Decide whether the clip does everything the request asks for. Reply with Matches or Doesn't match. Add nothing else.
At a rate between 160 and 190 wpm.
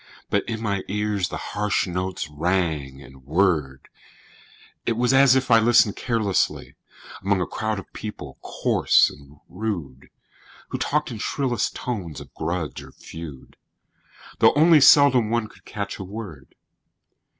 Doesn't match